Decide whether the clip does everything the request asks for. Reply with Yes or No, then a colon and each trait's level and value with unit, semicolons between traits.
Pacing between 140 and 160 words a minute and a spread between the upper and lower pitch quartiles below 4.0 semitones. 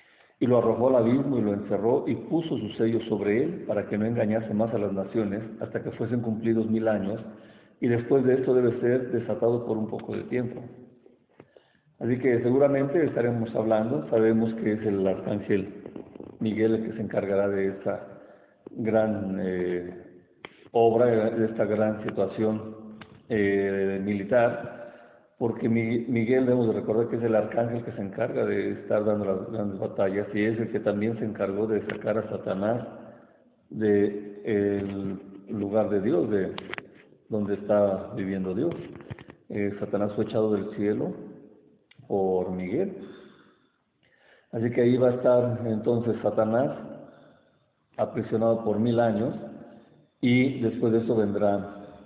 Yes: average, 150 wpm; narrow, 2.4 semitones